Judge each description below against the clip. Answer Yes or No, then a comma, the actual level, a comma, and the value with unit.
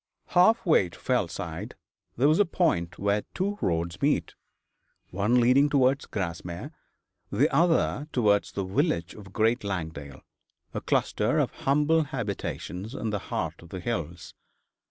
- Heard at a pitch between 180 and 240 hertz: No, low, 110 Hz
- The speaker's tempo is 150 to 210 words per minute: No, average, 140 wpm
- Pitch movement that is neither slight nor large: No, wide, 8.2 semitones